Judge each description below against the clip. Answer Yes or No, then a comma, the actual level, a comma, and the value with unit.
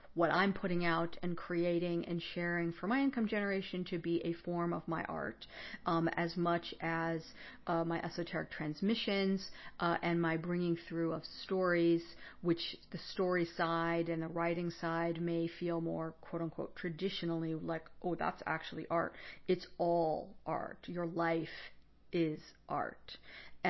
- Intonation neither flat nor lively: No, narrow, 1.0 semitones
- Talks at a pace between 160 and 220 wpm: No, average, 150 wpm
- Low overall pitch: No, medium, 170 Hz